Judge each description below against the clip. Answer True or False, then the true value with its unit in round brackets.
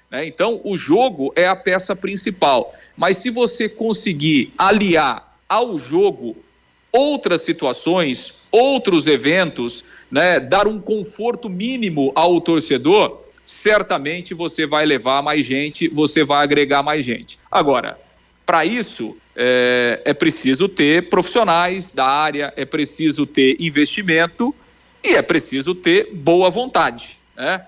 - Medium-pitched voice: True (175 Hz)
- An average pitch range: False (6.2 semitones)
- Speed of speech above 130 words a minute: False (125 wpm)